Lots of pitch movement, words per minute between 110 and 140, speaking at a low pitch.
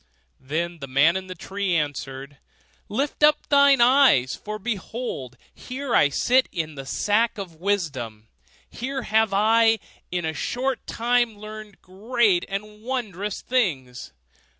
No: wide, 7.0 semitones; slow, 135 wpm; high, 205 Hz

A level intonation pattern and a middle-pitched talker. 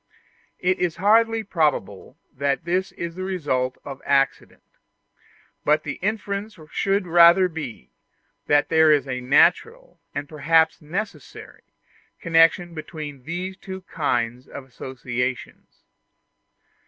No: average, 5.1 semitones; medium, 160 Hz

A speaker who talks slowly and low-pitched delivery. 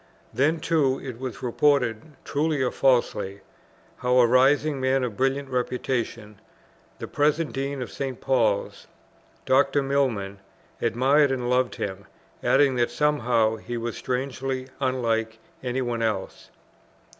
Yes: slow, 130 wpm; low, 130 Hz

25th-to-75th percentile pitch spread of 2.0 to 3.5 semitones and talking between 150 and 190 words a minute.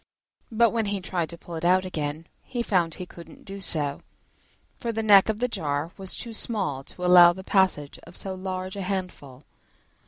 No: average, 3.2 semitones; fast, 205 wpm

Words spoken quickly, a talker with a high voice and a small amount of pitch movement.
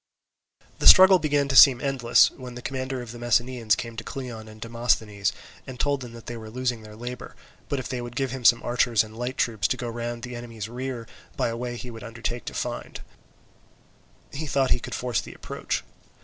No: fast, 220 wpm; low, 120 Hz; narrow, 2.0 semitones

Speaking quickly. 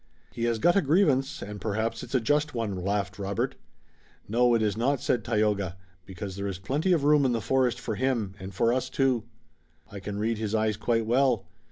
Yes: fast, 210 wpm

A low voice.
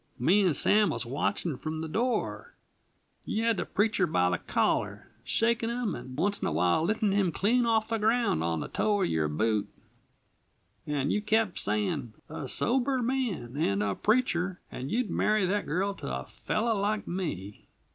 No: high, 190 Hz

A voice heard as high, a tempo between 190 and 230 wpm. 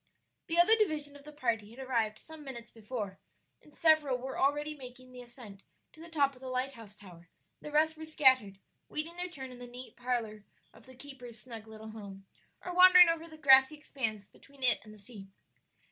Yes: very high, 260 Hz; average, 200 wpm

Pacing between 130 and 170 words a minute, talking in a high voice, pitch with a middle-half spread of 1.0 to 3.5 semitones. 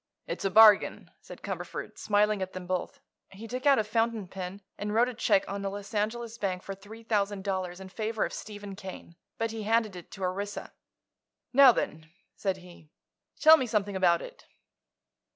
No: average, 190 wpm; high, 205 Hz; average, 2.8 semitones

